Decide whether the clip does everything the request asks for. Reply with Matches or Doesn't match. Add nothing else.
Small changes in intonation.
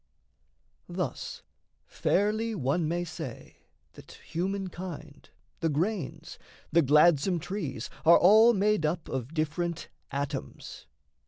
Doesn't match